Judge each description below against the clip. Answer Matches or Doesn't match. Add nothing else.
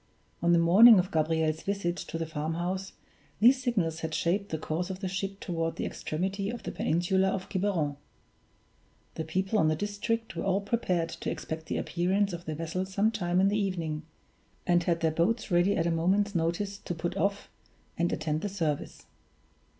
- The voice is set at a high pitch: Doesn't match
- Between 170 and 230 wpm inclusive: Matches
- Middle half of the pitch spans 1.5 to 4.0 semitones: Matches